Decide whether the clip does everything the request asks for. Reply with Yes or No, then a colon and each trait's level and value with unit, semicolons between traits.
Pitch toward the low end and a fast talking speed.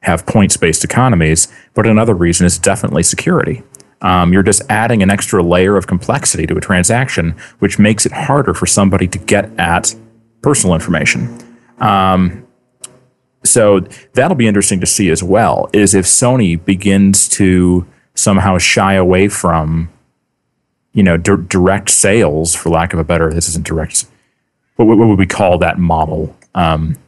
No: very low, 95 Hz; average, 155 wpm